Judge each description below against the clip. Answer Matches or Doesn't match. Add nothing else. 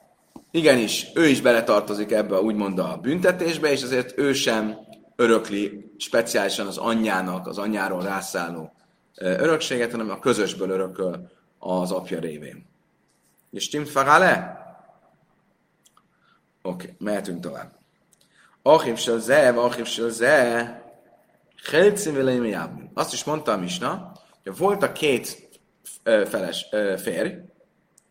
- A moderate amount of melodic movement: Matches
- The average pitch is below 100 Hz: Doesn't match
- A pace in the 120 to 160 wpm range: Doesn't match